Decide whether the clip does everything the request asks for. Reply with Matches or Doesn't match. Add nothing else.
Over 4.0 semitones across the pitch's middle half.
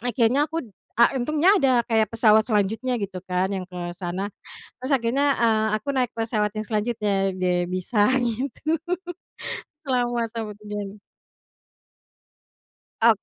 Doesn't match